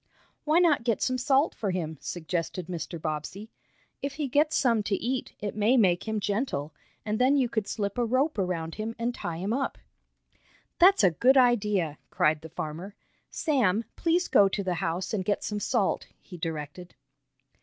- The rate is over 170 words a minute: Yes, average, 180 wpm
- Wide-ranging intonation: Yes, wide, 6.3 semitones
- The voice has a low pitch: No, high, 210 Hz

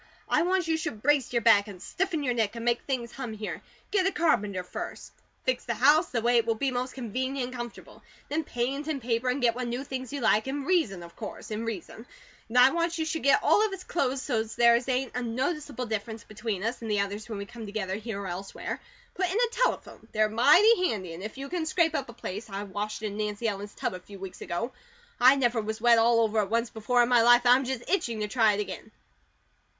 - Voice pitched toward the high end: Yes, high, 240 Hz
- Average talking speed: No, fast, 250 wpm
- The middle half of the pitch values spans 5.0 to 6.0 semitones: No, average, 4.0 semitones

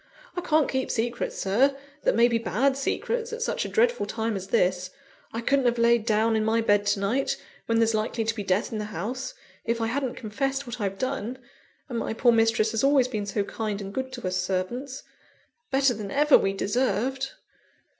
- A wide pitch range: No, average, 4.0 semitones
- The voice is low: No, high, 230 Hz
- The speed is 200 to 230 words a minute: Yes, fast, 205 wpm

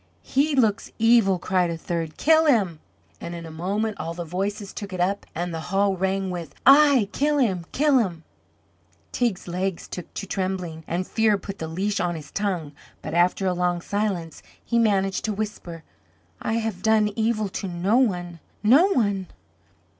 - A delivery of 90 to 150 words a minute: No, average, 175 wpm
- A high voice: Yes, high, 195 Hz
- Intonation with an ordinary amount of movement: Yes, average, 3.9 semitones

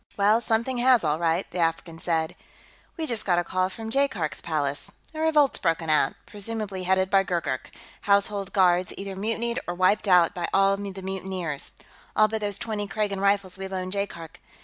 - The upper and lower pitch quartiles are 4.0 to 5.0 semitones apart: No, average, 3.3 semitones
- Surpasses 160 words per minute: Yes, average, 175 wpm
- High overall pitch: Yes, high, 195 Hz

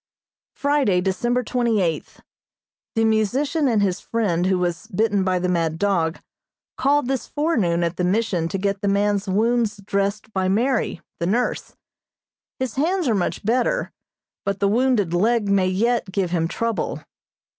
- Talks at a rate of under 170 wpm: Yes, average, 155 wpm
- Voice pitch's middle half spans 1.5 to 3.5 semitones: No, average, 4.4 semitones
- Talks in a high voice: Yes, high, 205 Hz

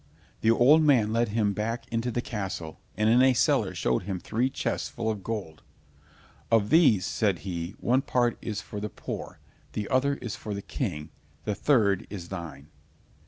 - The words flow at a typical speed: Yes, average, 180 wpm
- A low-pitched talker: Yes, low, 110 Hz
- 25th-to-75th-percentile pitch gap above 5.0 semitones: No, average, 3.6 semitones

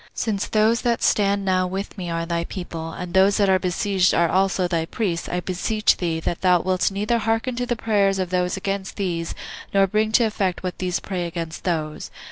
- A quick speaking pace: Yes, fast, 210 wpm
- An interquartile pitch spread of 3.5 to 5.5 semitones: No, average, 2.7 semitones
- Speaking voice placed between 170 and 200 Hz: Yes, high, 190 Hz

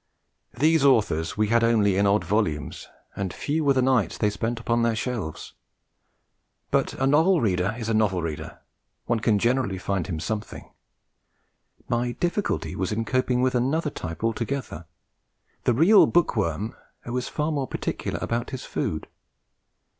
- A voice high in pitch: No, low, 115 Hz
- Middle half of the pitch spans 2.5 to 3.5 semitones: No, average, 4.4 semitones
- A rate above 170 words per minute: No, average, 155 wpm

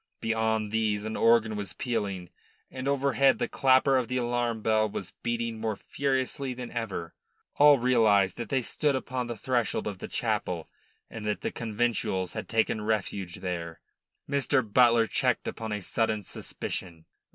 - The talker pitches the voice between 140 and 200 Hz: No, low, 115 Hz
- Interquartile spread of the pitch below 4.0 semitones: Yes, average, 3.4 semitones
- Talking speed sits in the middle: Yes, average, 160 wpm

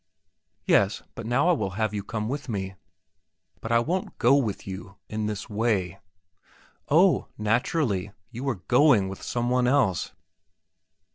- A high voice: No, low, 115 Hz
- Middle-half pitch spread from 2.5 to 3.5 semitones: No, average, 4.1 semitones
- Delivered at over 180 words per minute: No, average, 150 wpm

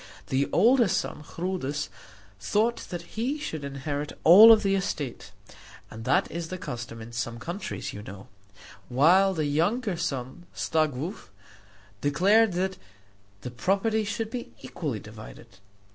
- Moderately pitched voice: Yes, medium, 165 Hz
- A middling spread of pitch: No, wide, 7.1 semitones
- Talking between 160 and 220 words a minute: No, slow, 135 wpm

